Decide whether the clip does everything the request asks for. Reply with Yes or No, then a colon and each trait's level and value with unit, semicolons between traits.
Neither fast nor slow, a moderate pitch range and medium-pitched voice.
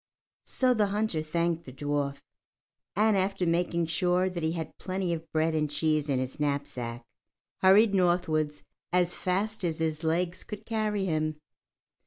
Yes: average, 155 wpm; average, 3.5 semitones; medium, 170 Hz